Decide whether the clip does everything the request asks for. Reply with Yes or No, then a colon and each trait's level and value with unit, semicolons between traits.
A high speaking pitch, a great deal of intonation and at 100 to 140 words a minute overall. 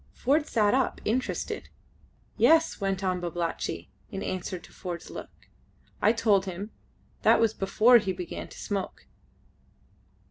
No: high, 200 Hz; average, 3.7 semitones; slow, 135 wpm